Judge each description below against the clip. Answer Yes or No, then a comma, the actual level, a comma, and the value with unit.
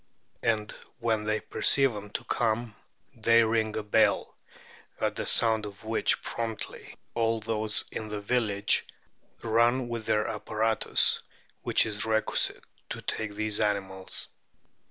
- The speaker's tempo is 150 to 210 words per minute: No, slow, 135 wpm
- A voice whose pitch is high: No, low, 110 Hz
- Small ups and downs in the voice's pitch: Yes, narrow, 1.4 semitones